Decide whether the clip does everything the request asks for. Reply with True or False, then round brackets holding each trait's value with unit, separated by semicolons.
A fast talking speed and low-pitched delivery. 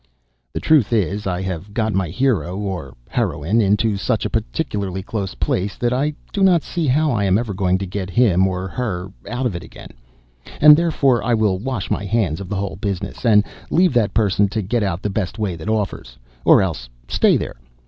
True (210 wpm; 100 Hz)